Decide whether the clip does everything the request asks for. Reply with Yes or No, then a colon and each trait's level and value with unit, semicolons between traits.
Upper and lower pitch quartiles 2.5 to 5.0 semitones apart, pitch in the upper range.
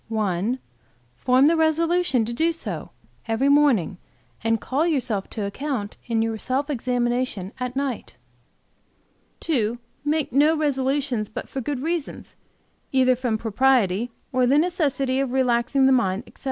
Yes: average, 4.0 semitones; very high, 255 Hz